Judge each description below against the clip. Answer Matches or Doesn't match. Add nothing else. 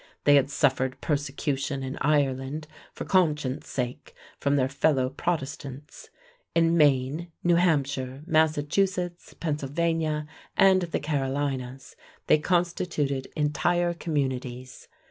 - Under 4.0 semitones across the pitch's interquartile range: Matches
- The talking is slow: Matches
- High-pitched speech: Doesn't match